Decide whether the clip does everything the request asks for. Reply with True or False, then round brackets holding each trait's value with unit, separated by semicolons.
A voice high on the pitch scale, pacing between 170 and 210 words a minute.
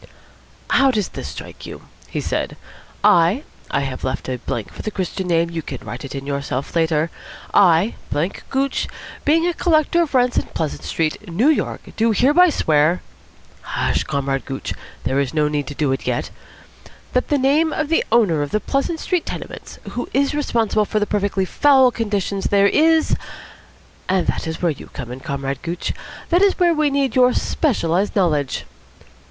True (195 Hz; 185 wpm)